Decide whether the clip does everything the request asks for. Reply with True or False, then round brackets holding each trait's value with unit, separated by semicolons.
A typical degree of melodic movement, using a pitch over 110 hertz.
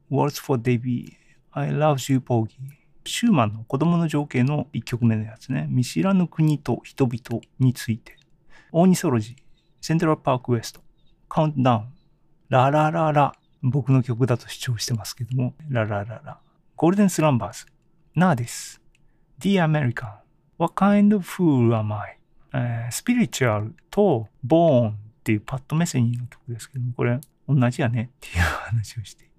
True (4.8 semitones; 135 Hz)